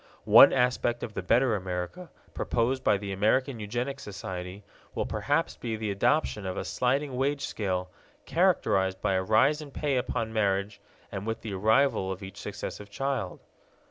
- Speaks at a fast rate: No, average, 165 wpm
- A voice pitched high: No, low, 110 Hz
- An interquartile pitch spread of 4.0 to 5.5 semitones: Yes, average, 5.0 semitones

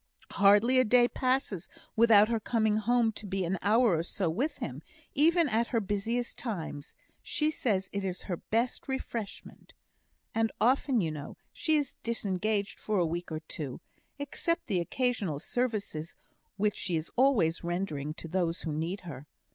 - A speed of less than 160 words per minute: No, average, 165 wpm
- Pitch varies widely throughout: Yes, wide, 5.7 semitones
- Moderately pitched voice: No, high, 210 Hz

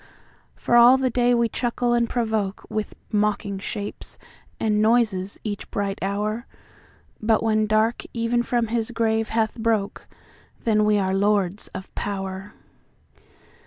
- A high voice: Yes, high, 215 Hz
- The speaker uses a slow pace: Yes, slow, 125 wpm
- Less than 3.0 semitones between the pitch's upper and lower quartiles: Yes, narrow, 2.4 semitones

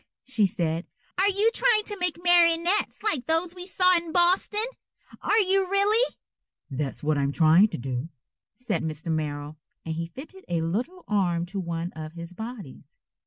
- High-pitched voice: Yes, high, 225 Hz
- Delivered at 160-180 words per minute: Yes, average, 170 wpm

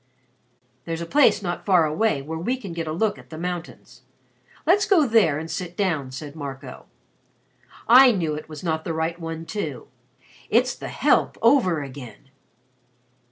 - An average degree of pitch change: Yes, average, 4.8 semitones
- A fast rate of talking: No, average, 165 wpm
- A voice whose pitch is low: No, medium, 165 Hz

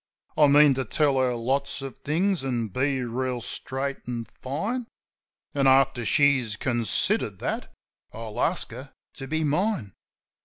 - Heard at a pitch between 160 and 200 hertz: No, low, 135 Hz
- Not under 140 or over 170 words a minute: Yes, average, 145 wpm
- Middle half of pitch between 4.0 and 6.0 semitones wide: No, average, 2.9 semitones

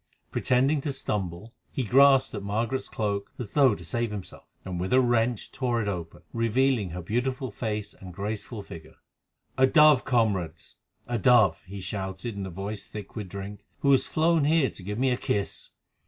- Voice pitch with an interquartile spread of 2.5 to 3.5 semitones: No, average, 4.7 semitones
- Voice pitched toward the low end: Yes, low, 110 Hz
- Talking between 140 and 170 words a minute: No, average, 180 wpm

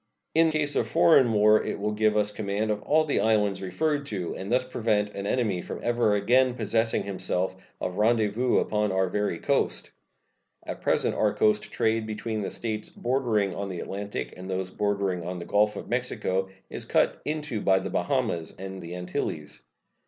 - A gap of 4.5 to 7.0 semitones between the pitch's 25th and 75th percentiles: No, average, 3.5 semitones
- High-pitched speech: No, low, 105 Hz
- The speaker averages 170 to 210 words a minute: Yes, average, 180 wpm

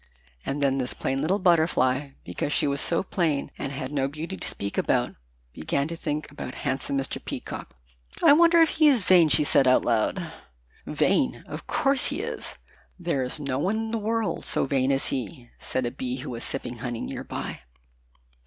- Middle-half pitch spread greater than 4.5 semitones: Yes, average, 5.1 semitones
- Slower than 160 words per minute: No, average, 195 wpm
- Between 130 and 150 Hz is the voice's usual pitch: Yes, medium, 140 Hz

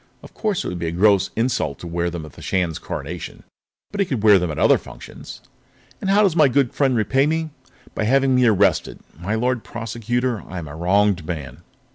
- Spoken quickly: Yes, fast, 215 wpm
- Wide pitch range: Yes, wide, 6.8 semitones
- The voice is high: No, low, 105 Hz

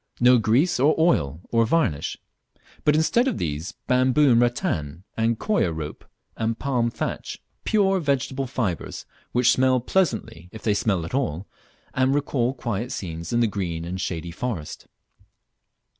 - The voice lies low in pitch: Yes, low, 120 Hz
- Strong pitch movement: Yes, wide, 7.2 semitones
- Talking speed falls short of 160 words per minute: Yes, average, 150 wpm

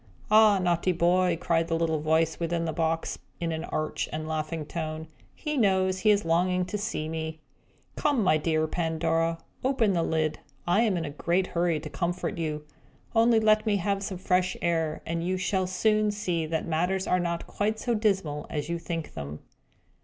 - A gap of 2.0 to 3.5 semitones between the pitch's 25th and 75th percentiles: Yes, average, 3.0 semitones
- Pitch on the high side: No, medium, 170 Hz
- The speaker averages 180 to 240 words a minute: Yes, average, 190 wpm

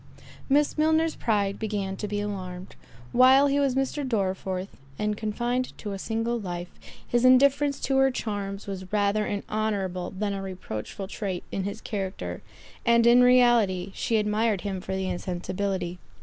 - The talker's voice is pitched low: No, high, 210 Hz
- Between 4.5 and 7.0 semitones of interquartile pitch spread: No, average, 3.9 semitones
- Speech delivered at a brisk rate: No, average, 160 wpm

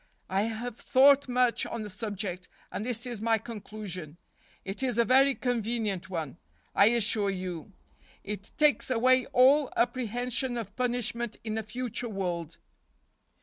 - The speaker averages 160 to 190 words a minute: No, average, 145 wpm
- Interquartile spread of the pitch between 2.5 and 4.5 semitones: Yes, average, 3.7 semitones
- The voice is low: No, high, 225 Hz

